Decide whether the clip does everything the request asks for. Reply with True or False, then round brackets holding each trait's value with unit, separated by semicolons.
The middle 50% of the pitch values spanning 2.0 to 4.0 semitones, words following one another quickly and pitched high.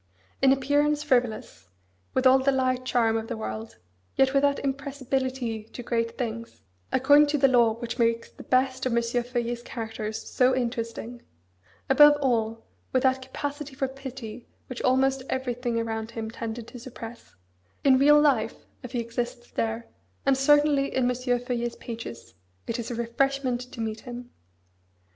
False (2.5 semitones; 160 wpm; 245 Hz)